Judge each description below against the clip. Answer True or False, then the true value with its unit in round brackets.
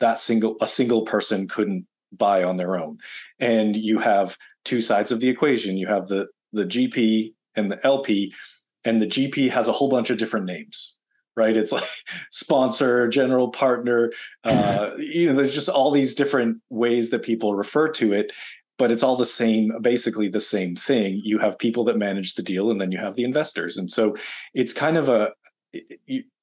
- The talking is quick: False (195 wpm)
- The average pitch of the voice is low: True (115 Hz)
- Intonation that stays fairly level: False (3.8 semitones)